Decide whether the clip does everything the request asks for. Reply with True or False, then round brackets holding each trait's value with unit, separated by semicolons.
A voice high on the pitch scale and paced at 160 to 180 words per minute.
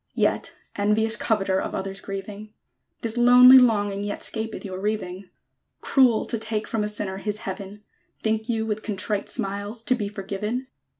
True (210 Hz; 165 wpm)